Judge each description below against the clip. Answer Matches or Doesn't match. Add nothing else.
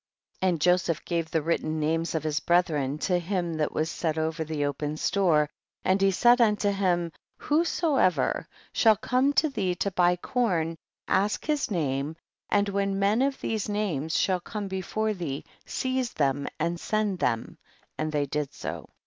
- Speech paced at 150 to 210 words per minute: Matches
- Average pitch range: Matches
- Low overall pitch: Doesn't match